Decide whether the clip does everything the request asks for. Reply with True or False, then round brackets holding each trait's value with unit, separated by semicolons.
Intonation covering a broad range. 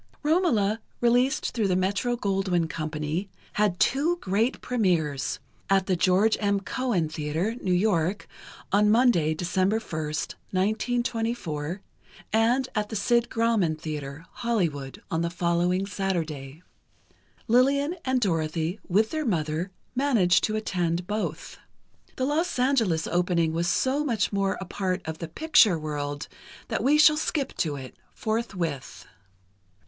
True (6.0 semitones)